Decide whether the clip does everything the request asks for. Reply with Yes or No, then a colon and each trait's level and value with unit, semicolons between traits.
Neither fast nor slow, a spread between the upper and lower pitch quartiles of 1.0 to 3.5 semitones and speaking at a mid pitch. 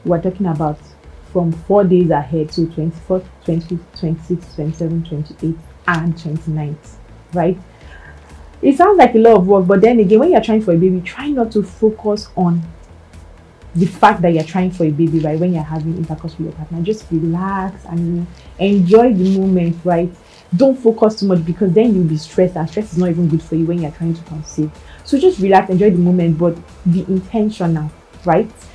Yes: average, 195 wpm; average, 3.2 semitones; medium, 175 Hz